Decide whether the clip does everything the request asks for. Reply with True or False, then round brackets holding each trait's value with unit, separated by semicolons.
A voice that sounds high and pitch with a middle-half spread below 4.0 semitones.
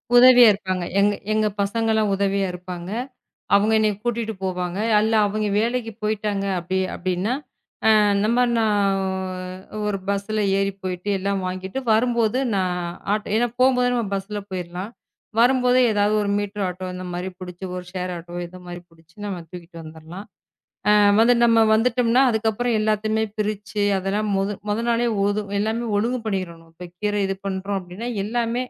True (205 Hz; 3.3 semitones)